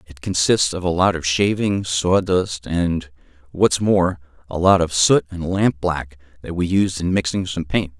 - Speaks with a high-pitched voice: No, very low, 85 Hz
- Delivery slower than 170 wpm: No, average, 180 wpm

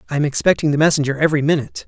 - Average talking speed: No, fast, 225 wpm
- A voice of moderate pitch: Yes, medium, 150 Hz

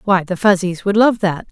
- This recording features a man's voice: No, female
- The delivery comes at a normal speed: No, fast, 235 wpm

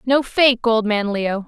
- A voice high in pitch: Yes, high, 230 Hz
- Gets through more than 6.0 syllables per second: No, 3.8 syllables/s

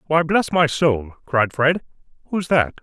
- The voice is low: No, medium, 145 Hz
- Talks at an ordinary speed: Yes, average, 170 wpm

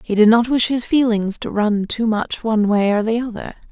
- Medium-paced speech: No, fast, 240 wpm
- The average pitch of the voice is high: Yes, high, 220 Hz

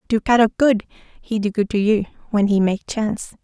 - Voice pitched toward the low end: No, high, 215 Hz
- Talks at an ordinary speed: No, fast, 210 wpm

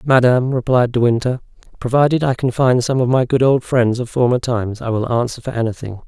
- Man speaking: Yes, male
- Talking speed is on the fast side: Yes, fast, 215 wpm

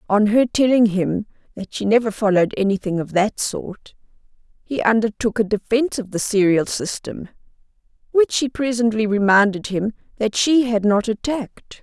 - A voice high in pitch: Yes, high, 220 Hz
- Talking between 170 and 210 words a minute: No, average, 150 wpm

